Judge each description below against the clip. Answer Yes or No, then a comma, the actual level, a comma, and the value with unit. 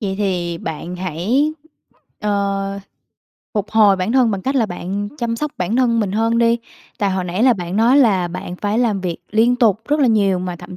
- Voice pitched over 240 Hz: No, high, 205 Hz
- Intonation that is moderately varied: Yes, average, 4.0 semitones